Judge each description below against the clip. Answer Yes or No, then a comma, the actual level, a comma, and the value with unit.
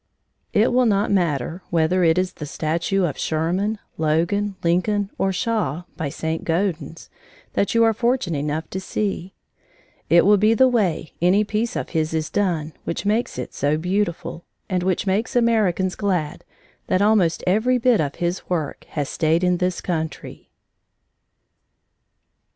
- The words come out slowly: No, average, 155 wpm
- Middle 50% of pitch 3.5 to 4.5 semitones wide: Yes, average, 4.2 semitones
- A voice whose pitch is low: No, medium, 180 Hz